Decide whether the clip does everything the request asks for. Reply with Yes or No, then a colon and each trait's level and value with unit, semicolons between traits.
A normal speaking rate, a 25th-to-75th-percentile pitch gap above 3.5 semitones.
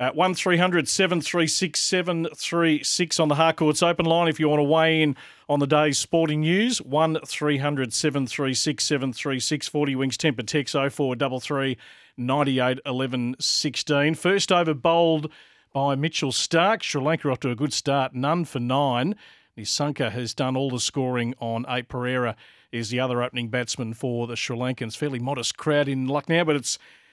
Yes: average, 170 wpm; average, 3.9 semitones